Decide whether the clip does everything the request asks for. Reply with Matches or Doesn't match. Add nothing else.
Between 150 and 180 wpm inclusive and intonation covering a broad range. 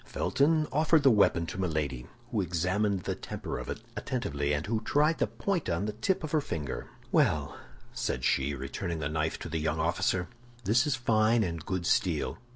Doesn't match